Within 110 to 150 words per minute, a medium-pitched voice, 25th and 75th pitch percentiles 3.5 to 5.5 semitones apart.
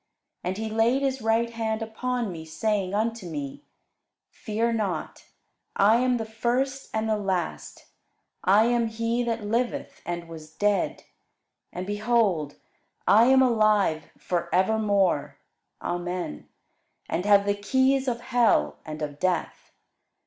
No: slow, 135 wpm; high, 215 Hz; average, 4.2 semitones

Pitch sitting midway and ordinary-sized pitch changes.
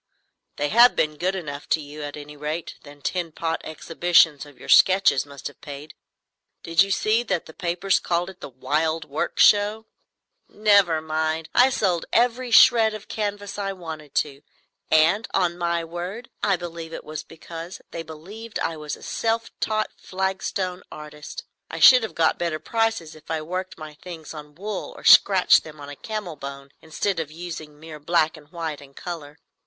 Yes: medium, 165 Hz; average, 4.2 semitones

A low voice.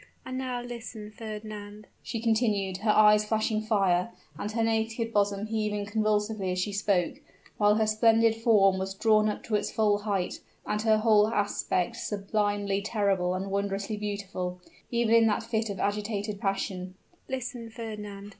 No: high, 210 Hz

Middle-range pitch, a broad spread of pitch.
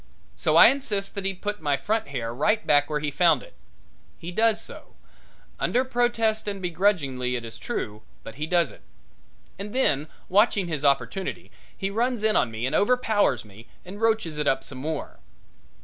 Yes: medium, 180 Hz; wide, 7.7 semitones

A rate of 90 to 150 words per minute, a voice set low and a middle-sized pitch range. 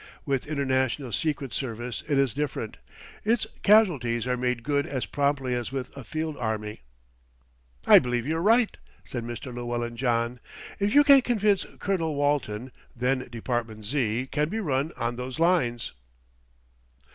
Yes: average, 145 wpm; low, 130 Hz; average, 4.4 semitones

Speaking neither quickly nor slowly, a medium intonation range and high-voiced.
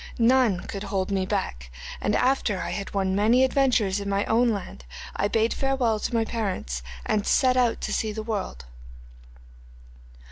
Yes: average, 170 wpm; average, 3.3 semitones; high, 210 Hz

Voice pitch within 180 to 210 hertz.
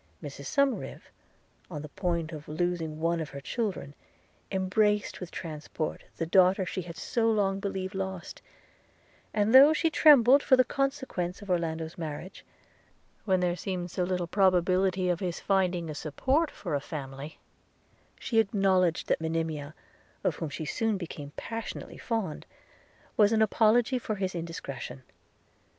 Yes: medium, 185 Hz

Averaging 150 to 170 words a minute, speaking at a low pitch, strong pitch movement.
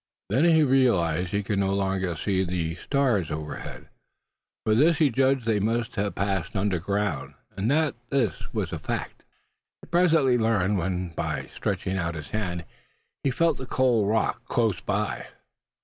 Yes: average, 165 wpm; low, 105 Hz; wide, 6.0 semitones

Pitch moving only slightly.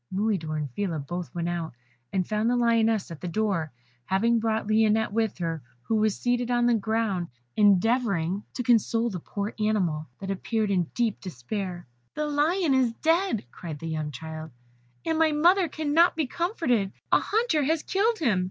No: wide, 5.6 semitones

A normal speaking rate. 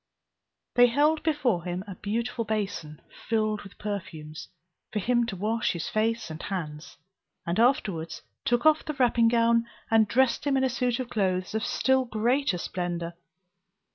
Yes: average, 160 wpm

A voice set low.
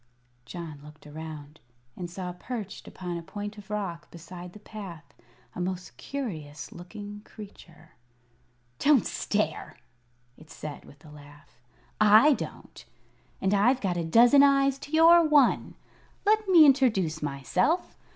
No: high, 190 Hz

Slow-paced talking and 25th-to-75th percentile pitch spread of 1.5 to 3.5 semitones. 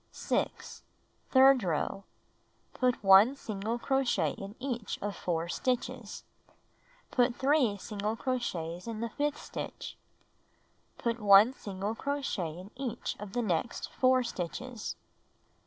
No: slow, 120 wpm; average, 4.5 semitones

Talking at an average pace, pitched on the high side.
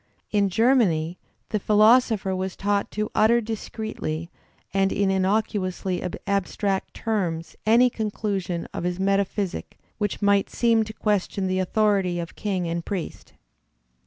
No: slow, 130 wpm; high, 200 Hz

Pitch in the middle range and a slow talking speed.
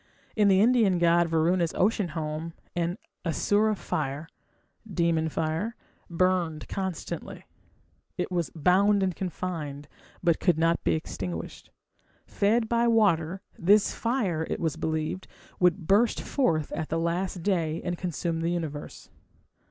Yes: medium, 175 Hz; slow, 130 wpm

